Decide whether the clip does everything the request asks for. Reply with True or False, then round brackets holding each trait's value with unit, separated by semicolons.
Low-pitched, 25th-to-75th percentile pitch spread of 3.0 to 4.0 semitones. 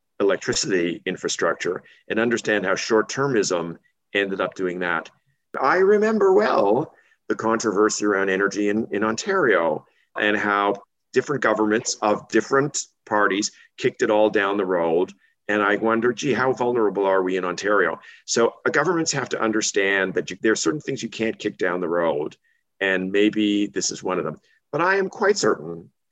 True (105 Hz; 3.3 semitones)